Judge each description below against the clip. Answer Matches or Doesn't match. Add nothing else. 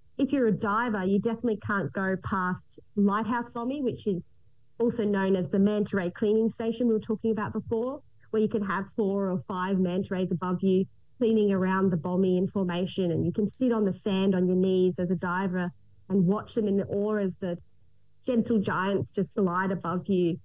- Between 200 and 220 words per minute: Matches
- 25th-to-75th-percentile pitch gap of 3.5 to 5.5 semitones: Doesn't match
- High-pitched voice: Matches